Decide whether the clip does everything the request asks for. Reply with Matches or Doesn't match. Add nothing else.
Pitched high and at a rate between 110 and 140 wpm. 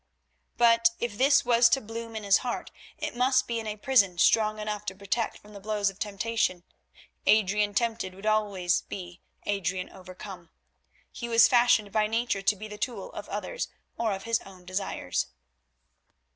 Doesn't match